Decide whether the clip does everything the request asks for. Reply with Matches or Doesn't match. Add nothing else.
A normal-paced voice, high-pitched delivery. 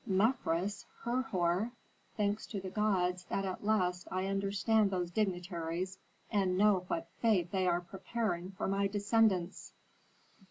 Doesn't match